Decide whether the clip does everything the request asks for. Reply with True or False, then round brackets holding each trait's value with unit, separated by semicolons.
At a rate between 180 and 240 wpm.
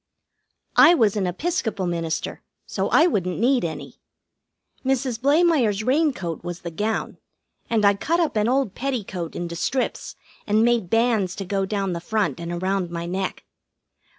False (155 wpm)